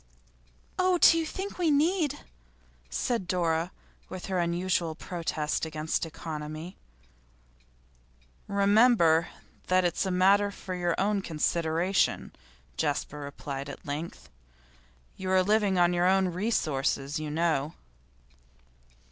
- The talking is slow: Yes, slow, 110 wpm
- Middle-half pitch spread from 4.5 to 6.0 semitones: No, average, 3.8 semitones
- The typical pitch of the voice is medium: Yes, medium, 175 Hz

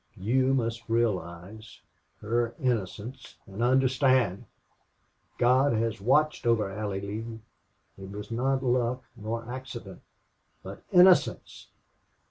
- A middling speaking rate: No, slow, 100 wpm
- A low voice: Yes, low, 115 Hz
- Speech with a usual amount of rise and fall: Yes, average, 3.6 semitones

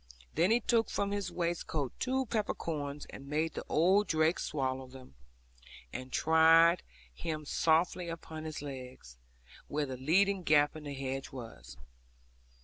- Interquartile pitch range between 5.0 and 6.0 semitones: No, average, 4.2 semitones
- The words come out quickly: No, average, 145 wpm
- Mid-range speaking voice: Yes, medium, 155 Hz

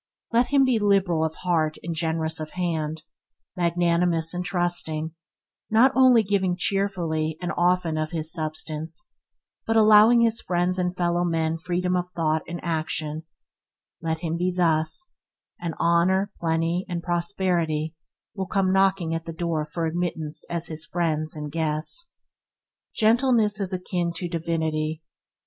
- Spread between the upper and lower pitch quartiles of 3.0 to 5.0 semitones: No, narrow, 2.6 semitones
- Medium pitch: Yes, medium, 170 Hz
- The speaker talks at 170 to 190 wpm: No, average, 145 wpm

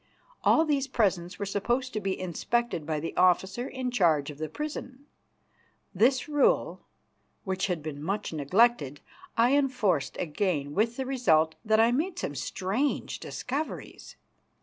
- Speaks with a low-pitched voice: No, high, 205 Hz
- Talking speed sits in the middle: Yes, average, 145 wpm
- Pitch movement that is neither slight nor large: No, wide, 7.5 semitones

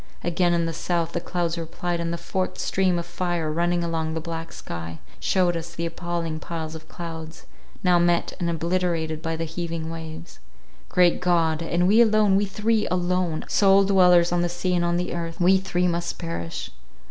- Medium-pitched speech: Yes, medium, 170 Hz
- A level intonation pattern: Yes, narrow, 1.5 semitones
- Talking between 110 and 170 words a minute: No, average, 180 wpm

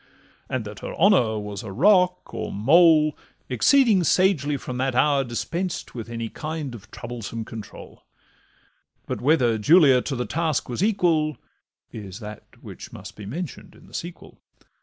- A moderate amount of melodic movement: No, wide, 6.6 semitones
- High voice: No, low, 135 Hz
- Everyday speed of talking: Yes, average, 155 wpm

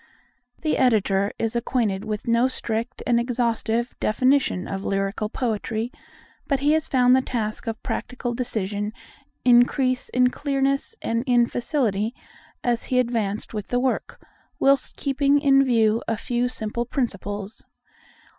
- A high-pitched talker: Yes, high, 240 Hz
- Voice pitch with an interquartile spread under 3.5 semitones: Yes, average, 2.9 semitones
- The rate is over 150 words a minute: No, slow, 135 wpm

